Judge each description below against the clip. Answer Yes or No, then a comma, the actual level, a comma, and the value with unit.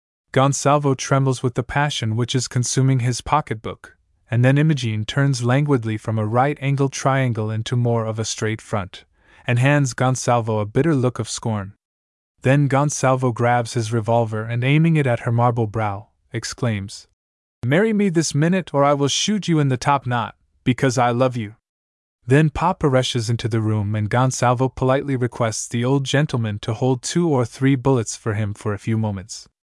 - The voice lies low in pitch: Yes, low, 125 Hz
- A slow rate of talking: No, average, 180 wpm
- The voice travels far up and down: No, average, 3.6 semitones